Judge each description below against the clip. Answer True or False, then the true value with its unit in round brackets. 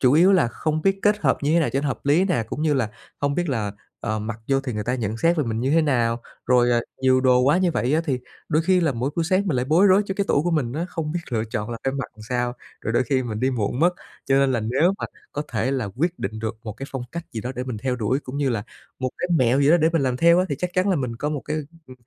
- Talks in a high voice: False (135 Hz)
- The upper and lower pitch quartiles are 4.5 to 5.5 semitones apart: True (5.2 semitones)